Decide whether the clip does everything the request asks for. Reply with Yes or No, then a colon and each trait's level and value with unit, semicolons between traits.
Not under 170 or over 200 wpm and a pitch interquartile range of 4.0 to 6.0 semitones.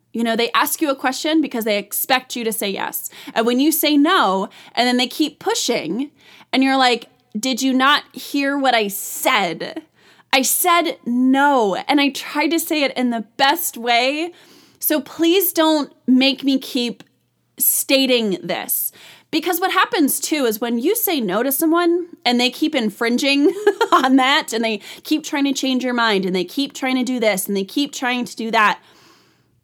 Yes: average, 190 wpm; average, 4.3 semitones